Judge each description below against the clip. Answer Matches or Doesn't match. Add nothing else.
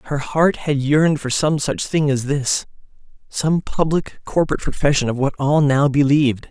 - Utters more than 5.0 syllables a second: Doesn't match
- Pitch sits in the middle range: Matches